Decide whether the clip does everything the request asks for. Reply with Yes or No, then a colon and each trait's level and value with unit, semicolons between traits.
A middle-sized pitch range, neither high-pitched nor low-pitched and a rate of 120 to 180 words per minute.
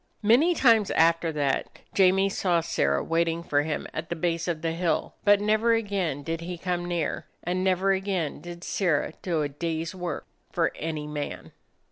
Yes: average, 3.0 semitones; medium, 170 Hz; average, 175 wpm